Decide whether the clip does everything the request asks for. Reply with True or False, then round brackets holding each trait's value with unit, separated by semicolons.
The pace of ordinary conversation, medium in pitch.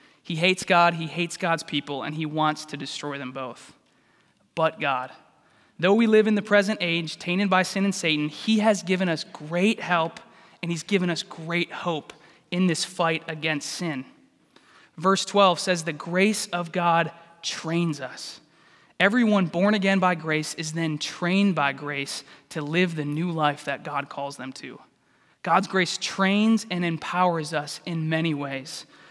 True (170 wpm; 170 Hz)